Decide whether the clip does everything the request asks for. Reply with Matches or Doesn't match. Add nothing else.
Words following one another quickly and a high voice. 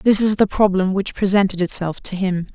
Matches